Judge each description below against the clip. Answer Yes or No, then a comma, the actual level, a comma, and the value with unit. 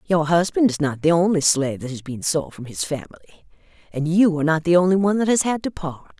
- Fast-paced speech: Yes, fast, 250 wpm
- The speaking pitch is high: No, medium, 165 Hz